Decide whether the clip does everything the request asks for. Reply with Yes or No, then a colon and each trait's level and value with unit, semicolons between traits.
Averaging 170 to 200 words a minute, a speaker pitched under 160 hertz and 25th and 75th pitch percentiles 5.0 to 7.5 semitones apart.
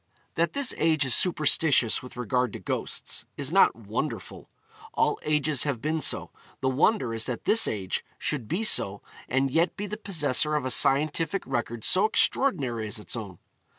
Yes: average, 175 wpm; medium, 140 Hz; wide, 5.4 semitones